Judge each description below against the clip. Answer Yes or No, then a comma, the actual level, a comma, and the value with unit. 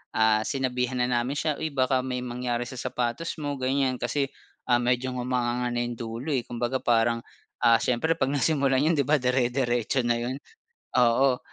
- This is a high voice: No, low, 125 Hz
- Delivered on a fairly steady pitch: Yes, narrow, 1.8 semitones